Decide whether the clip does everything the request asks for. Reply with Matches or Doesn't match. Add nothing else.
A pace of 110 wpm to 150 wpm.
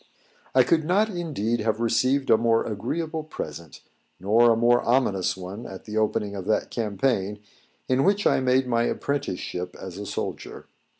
Doesn't match